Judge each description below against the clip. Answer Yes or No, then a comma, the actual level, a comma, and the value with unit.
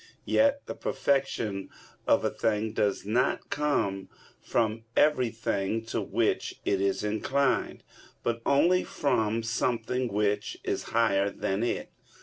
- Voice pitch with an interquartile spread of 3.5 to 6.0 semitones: Yes, average, 3.9 semitones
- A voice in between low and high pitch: No, low, 115 Hz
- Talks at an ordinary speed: No, slow, 125 wpm